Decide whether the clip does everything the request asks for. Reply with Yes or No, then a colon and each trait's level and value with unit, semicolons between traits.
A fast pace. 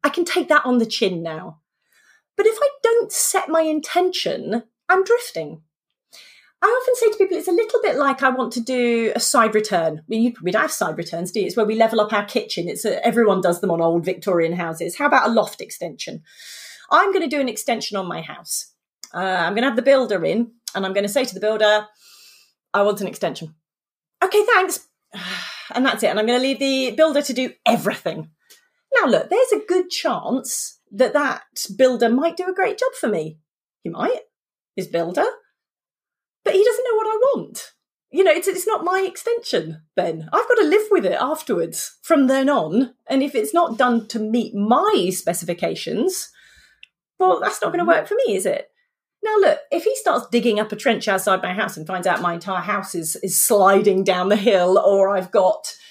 Yes: fast, 215 wpm